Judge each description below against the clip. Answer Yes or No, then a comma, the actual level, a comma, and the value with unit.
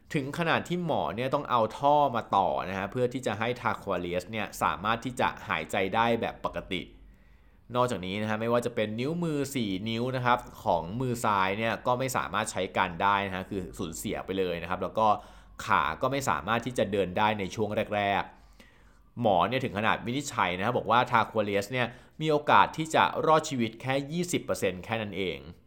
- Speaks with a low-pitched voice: Yes, low, 115 Hz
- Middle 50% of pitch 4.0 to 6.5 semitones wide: Yes, average, 4.5 semitones